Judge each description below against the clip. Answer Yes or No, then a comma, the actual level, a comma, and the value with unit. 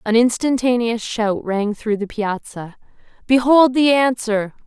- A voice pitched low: No, high, 230 Hz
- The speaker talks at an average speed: No, slow, 130 wpm